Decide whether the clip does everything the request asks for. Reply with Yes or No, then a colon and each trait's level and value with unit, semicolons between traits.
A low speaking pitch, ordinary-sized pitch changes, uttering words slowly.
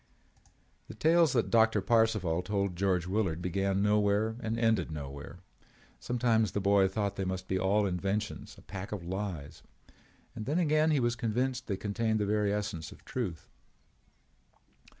No: low, 105 Hz; average, 3.1 semitones; average, 160 wpm